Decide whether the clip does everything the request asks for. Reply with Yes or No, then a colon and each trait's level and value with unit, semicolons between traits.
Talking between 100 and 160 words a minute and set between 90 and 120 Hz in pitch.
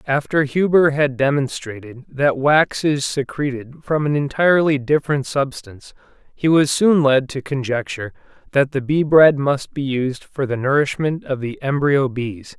No: average, 155 wpm; medium, 140 Hz